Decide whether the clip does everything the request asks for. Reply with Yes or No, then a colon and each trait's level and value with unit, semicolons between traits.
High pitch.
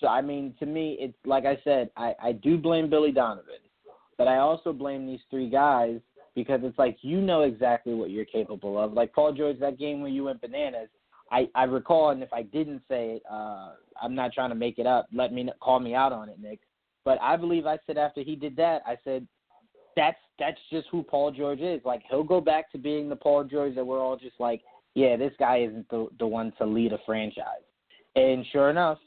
No: low, 135 Hz